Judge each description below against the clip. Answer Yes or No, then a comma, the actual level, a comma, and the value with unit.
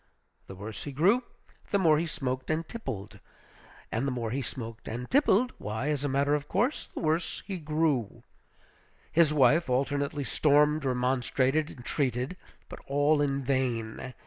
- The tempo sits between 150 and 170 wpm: Yes, average, 155 wpm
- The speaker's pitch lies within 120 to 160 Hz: Yes, medium, 140 Hz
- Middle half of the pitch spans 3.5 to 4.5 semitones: Yes, average, 3.8 semitones